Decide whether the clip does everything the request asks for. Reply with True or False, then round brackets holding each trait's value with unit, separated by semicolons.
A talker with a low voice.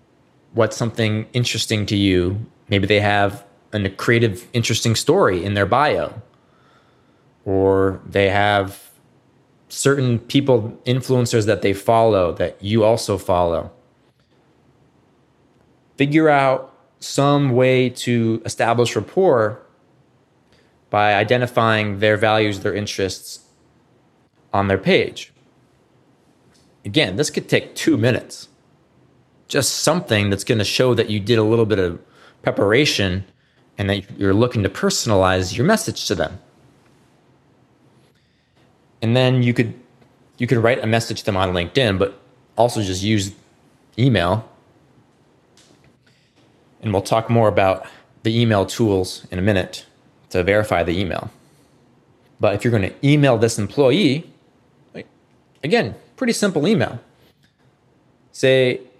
True (115 Hz)